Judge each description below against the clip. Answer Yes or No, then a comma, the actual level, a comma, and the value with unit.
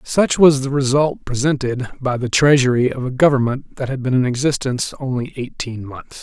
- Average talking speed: Yes, average, 185 wpm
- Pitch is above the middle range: No, low, 130 Hz